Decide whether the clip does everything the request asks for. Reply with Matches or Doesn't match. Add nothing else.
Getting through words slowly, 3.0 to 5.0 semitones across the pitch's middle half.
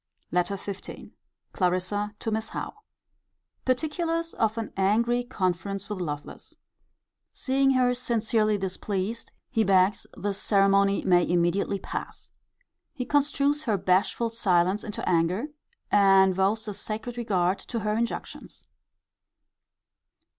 Matches